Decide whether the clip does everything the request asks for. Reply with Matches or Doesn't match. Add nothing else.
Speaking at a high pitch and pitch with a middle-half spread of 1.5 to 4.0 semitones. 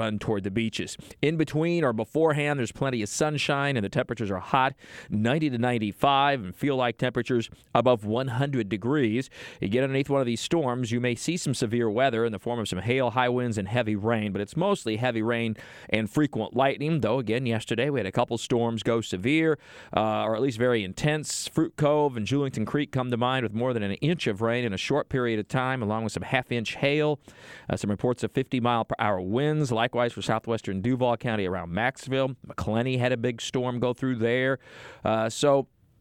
Doesn't match